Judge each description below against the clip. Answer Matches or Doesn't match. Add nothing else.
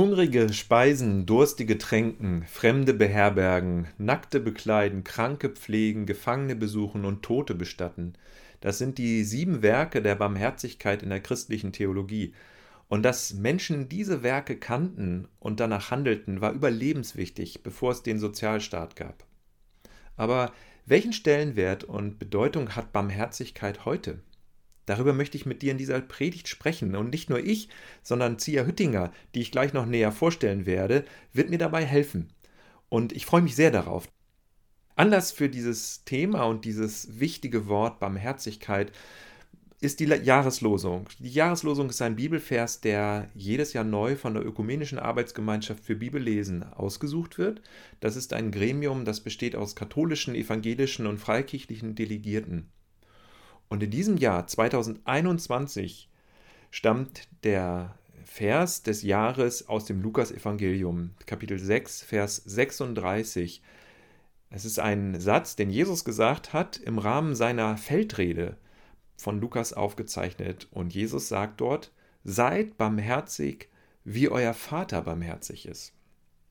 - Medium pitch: Doesn't match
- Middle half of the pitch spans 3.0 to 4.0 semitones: Doesn't match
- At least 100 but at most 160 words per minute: Matches